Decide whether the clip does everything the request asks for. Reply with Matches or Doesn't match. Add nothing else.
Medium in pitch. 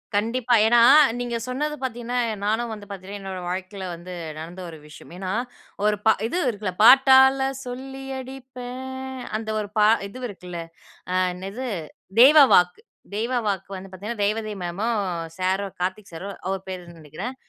Doesn't match